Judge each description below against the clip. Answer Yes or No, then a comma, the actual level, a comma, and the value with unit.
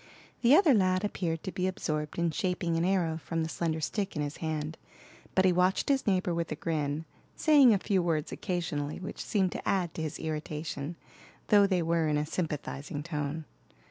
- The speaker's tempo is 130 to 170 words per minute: No, average, 195 wpm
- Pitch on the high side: No, medium, 170 Hz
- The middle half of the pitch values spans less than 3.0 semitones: No, average, 3.3 semitones